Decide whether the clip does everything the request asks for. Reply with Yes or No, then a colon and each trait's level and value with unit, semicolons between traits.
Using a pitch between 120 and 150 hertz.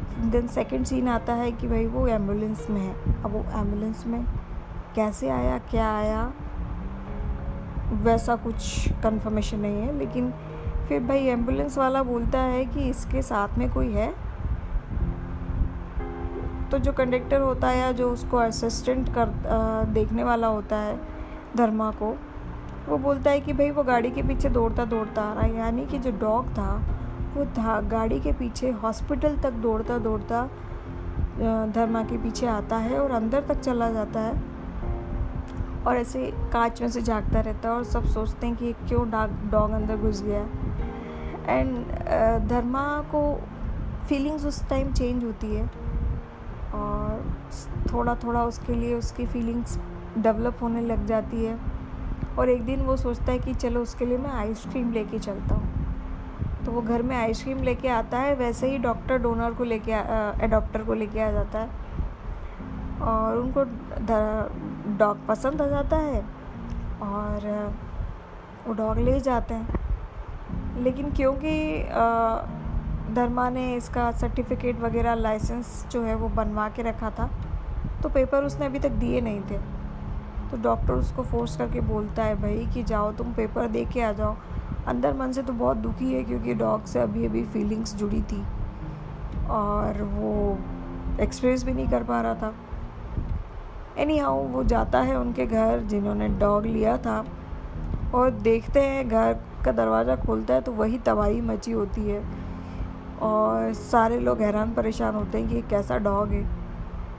No: high, 225 Hz